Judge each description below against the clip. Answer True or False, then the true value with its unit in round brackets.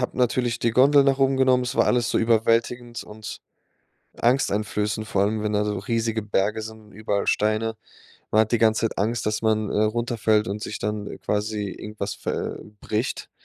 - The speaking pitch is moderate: False (110 Hz)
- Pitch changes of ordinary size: False (1.9 semitones)